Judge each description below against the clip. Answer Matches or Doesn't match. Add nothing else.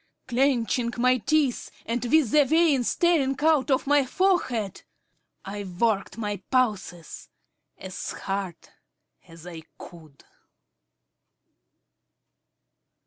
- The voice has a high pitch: Matches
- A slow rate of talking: Matches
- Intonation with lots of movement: Matches